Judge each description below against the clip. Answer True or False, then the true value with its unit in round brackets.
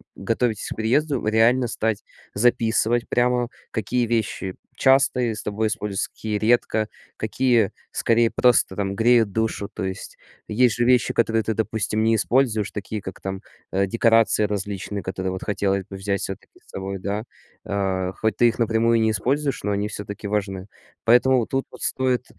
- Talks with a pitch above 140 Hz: False (110 Hz)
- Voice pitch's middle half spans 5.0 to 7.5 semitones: False (2.9 semitones)